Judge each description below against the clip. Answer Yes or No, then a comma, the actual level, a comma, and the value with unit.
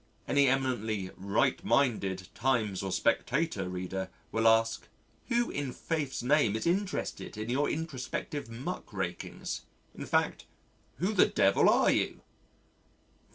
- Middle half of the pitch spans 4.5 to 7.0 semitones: Yes, wide, 5.6 semitones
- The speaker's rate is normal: No, slow, 125 wpm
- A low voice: Yes, low, 125 Hz